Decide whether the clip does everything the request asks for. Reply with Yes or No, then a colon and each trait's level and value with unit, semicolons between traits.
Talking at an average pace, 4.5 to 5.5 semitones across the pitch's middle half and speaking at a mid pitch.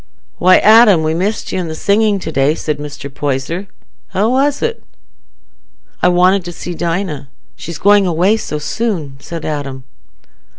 Yes: average, 155 wpm; average, 5.1 semitones; medium, 175 Hz